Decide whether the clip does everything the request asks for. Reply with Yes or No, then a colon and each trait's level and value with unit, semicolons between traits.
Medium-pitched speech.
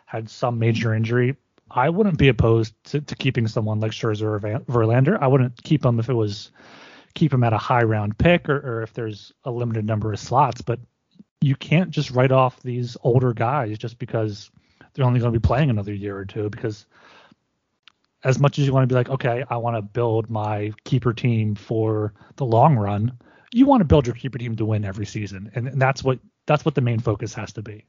No: low, 120 Hz